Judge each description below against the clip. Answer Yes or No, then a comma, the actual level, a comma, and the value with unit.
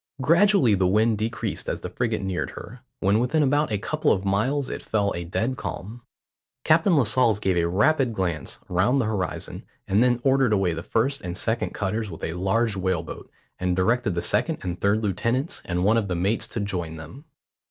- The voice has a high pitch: No, low, 105 Hz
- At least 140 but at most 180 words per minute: No, average, 200 wpm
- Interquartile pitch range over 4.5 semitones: Yes, average, 5.0 semitones